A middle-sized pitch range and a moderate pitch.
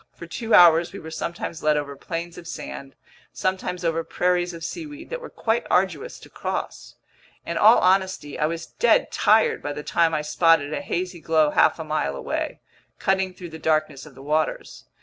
Yes: average, 3.2 semitones; medium, 165 Hz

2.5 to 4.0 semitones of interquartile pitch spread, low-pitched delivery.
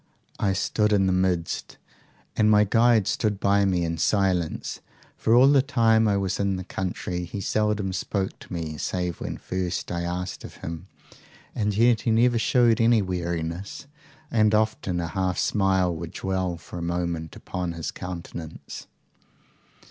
Yes: average, 3.5 semitones; very low, 95 Hz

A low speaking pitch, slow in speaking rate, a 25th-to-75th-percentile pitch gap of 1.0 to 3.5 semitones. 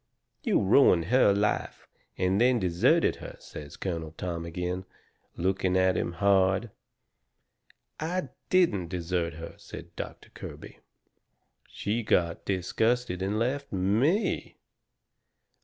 No: very low, 95 Hz; slow, 110 wpm; average, 4.5 semitones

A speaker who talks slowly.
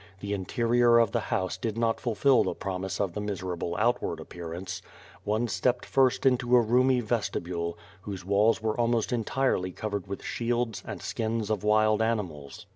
No: average, 165 wpm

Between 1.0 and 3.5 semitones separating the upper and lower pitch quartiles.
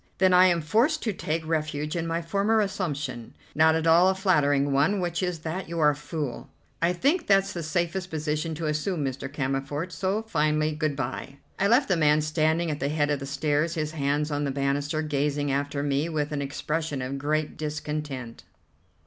Yes: average, 3.0 semitones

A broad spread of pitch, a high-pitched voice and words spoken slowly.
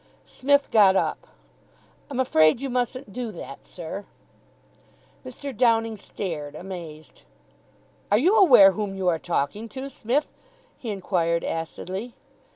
Yes: wide, 6.3 semitones; high, 210 Hz; slow, 125 wpm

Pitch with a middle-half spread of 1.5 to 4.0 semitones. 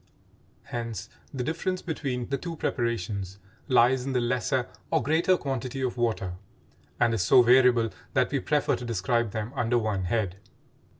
Yes: average, 2.8 semitones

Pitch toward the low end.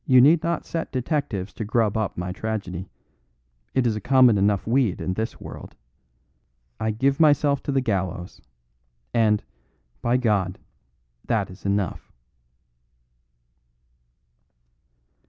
Yes: low, 110 Hz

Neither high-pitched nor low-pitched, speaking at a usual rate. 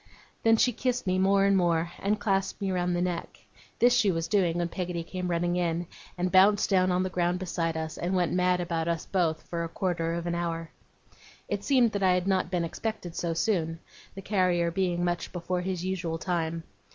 No: medium, 180 Hz; fast, 210 wpm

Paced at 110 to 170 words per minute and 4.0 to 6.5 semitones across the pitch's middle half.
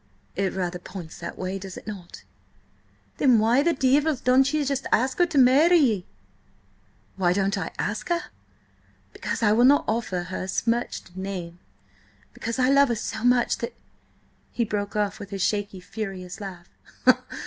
Yes: average, 165 wpm; average, 5.2 semitones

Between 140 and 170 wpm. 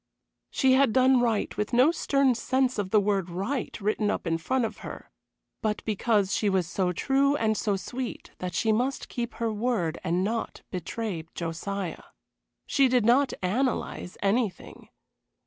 Yes: average, 165 wpm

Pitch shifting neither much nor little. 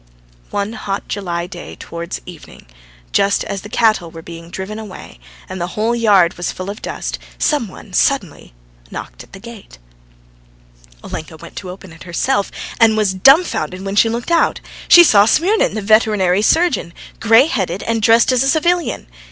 Yes: average, 4.2 semitones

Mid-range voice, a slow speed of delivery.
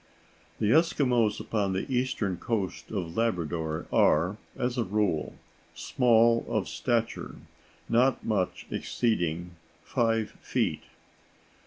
No: low, 110 Hz; slow, 105 wpm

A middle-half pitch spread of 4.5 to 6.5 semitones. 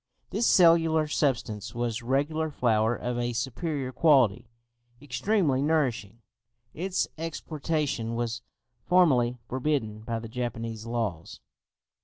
Yes: average, 5.2 semitones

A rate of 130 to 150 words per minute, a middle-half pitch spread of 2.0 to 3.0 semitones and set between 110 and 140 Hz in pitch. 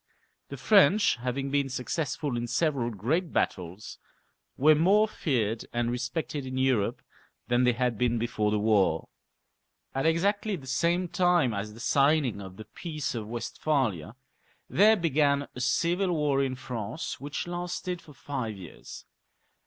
No: average, 145 wpm; wide, 5.6 semitones; low, 135 Hz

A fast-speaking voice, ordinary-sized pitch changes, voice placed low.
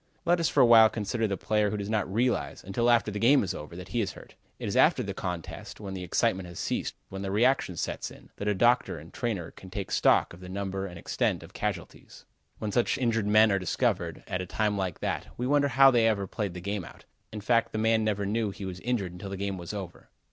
Yes: fast, 250 wpm; average, 3.2 semitones; low, 105 Hz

